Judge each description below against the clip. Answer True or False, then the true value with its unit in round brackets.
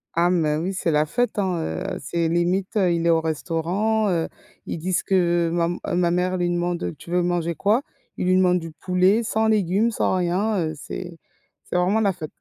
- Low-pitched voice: False (180 Hz)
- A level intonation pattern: True (2.2 semitones)